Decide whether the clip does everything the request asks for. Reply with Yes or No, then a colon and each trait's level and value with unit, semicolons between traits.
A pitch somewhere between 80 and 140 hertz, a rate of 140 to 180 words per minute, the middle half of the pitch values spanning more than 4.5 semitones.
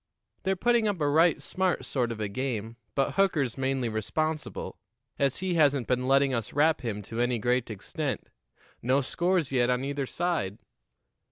Yes: low, 135 Hz; average, 170 wpm; average, 4.9 semitones